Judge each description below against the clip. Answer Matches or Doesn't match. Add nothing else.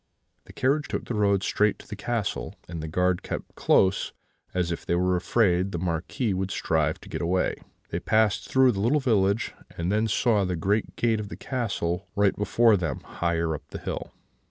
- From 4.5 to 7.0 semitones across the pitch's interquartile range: Doesn't match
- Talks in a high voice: Doesn't match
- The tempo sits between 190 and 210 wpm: Matches